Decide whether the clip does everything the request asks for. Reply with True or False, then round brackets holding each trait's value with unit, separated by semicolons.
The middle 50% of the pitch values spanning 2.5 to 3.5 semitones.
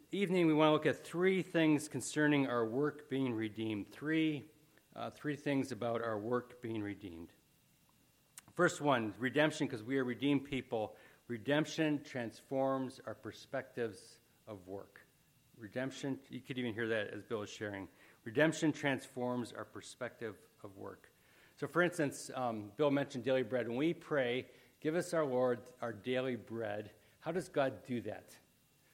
False (4.2 semitones)